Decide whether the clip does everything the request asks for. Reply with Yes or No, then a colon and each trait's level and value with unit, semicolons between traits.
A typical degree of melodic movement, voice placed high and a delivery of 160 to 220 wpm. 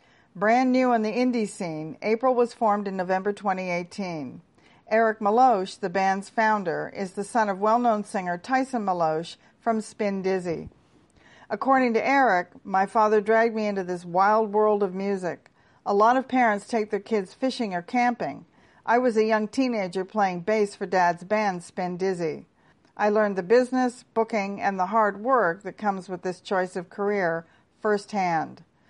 Yes: average, 3.1 semitones; high, 205 Hz; average, 170 wpm